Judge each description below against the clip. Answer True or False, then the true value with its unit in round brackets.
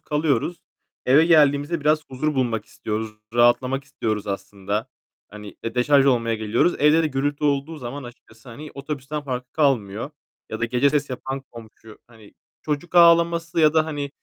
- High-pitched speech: False (135 Hz)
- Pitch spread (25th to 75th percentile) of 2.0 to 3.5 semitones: False (4.4 semitones)